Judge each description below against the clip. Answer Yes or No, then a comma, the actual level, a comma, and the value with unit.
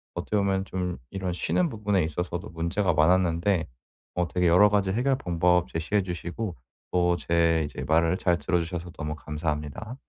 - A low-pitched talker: Yes, very low, 90 Hz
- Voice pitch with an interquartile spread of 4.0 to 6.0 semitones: No, average, 2.7 semitones